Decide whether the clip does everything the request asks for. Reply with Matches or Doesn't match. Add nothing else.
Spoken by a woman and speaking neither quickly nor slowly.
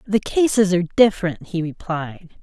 Matches